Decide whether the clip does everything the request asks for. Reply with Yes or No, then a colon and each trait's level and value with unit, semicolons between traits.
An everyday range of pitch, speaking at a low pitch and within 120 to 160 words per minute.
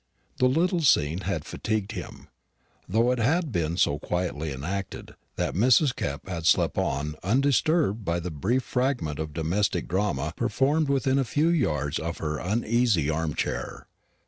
No: wide, 8.2 semitones; low, 100 Hz; average, 155 wpm